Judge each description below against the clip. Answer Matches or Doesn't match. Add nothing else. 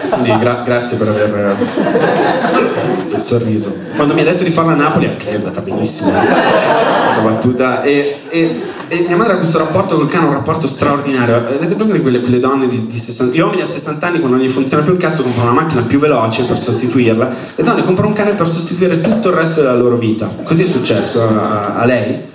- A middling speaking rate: Doesn't match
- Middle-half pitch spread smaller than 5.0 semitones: Doesn't match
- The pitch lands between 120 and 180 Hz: Matches